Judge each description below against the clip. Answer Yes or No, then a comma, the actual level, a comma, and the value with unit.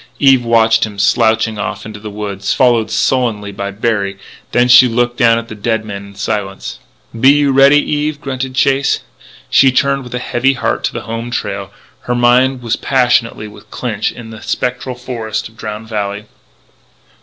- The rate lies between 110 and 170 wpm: No, average, 180 wpm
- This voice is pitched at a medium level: No, low, 115 Hz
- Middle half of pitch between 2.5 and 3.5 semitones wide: Yes, average, 3.0 semitones